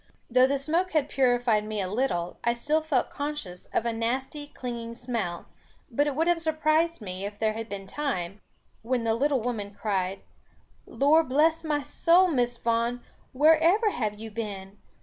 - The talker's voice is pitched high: Yes, high, 245 Hz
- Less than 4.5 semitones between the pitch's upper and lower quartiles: No, wide, 5.6 semitones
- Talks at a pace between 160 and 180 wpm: Yes, average, 175 wpm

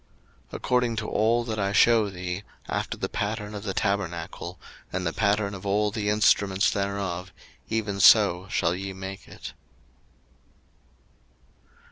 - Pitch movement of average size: No, narrow, 2.0 semitones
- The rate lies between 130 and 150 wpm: Yes, average, 140 wpm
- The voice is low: Yes, low, 100 Hz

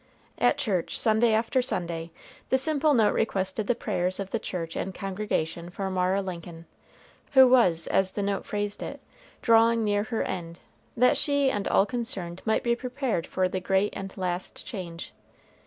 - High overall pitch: Yes, high, 200 Hz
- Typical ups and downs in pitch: Yes, average, 4.2 semitones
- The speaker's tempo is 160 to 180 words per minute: Yes, average, 170 wpm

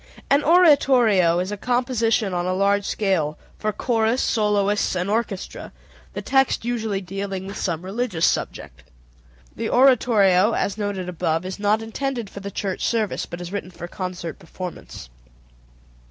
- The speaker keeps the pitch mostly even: No, average, 3.7 semitones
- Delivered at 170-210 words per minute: No, average, 150 wpm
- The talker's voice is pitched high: Yes, high, 200 Hz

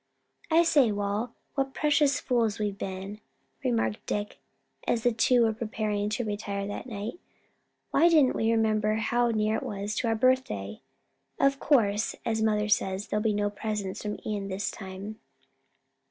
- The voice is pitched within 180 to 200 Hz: No, high, 215 Hz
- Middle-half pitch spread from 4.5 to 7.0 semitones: No, average, 2.7 semitones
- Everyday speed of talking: Yes, average, 160 wpm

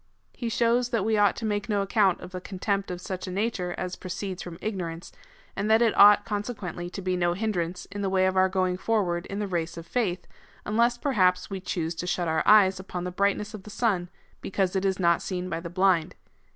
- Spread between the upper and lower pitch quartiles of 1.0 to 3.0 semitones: Yes, narrow, 2.6 semitones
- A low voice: No, high, 190 Hz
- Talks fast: Yes, fast, 230 wpm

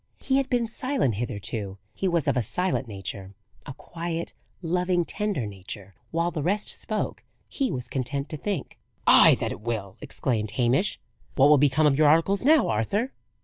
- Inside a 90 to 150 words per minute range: No, average, 175 wpm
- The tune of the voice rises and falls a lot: Yes, wide, 8.9 semitones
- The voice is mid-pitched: Yes, medium, 150 Hz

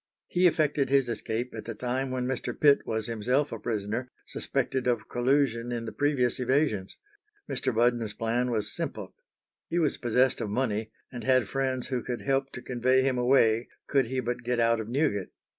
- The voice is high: No, low, 125 Hz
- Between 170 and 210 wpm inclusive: Yes, average, 185 wpm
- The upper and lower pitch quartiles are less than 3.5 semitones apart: Yes, narrow, 2.5 semitones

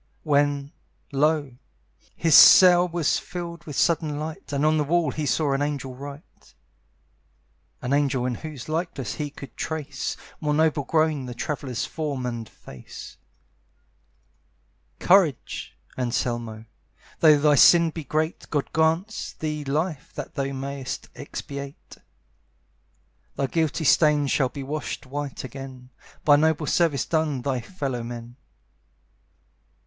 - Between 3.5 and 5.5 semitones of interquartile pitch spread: No, average, 2.9 semitones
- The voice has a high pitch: No, medium, 145 Hz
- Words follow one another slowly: Yes, slow, 130 wpm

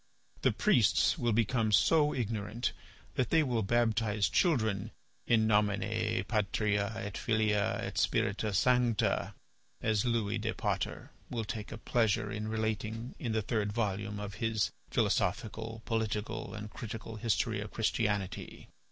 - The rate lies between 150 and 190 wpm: No, slow, 135 wpm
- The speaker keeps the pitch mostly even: Yes, narrow, 1.8 semitones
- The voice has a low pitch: Yes, low, 110 Hz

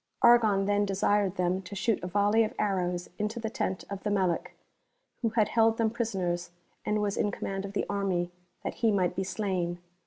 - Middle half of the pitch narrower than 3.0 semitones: Yes, narrow, 2.5 semitones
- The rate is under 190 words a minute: No, fast, 205 wpm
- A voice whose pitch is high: Yes, high, 200 Hz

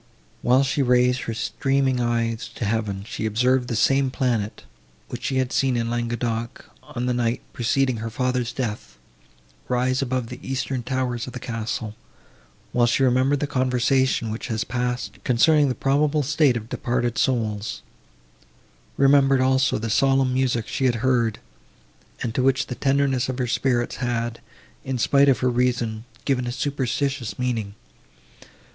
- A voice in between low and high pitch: No, low, 125 Hz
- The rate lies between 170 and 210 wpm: No, average, 155 wpm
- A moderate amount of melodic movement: No, narrow, 2.2 semitones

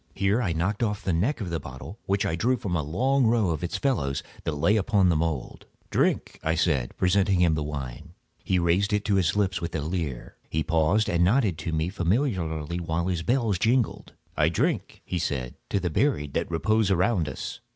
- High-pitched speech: No, very low, 90 Hz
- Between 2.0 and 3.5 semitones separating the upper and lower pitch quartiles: No, average, 4.4 semitones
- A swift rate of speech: Yes, fast, 210 wpm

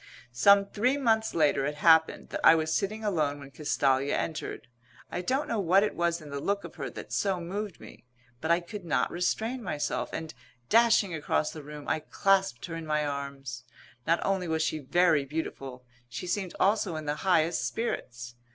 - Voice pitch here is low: No, medium, 165 Hz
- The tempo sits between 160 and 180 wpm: No, average, 190 wpm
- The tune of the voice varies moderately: Yes, average, 5.0 semitones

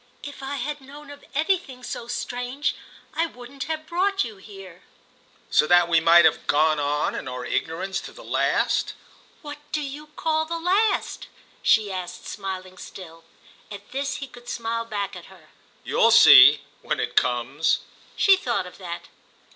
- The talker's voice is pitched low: No, high, 230 Hz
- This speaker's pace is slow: No, average, 165 wpm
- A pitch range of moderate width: No, wide, 8.7 semitones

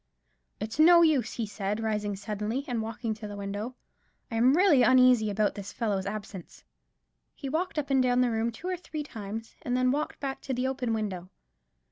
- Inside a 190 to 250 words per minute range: Yes, average, 195 wpm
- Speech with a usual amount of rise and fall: Yes, average, 4.1 semitones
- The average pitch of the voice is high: Yes, high, 230 Hz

